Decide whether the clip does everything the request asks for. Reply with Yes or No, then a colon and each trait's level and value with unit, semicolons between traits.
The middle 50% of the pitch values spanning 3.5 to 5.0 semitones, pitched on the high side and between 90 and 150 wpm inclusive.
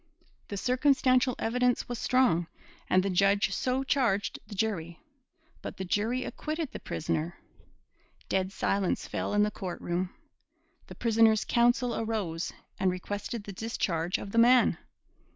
Yes: average, 4.7 semitones; high, 210 Hz; average, 140 wpm